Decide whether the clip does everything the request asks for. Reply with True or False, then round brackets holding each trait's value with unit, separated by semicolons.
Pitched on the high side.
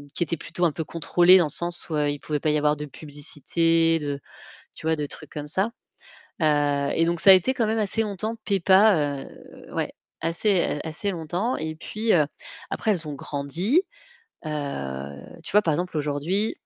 False (165 Hz)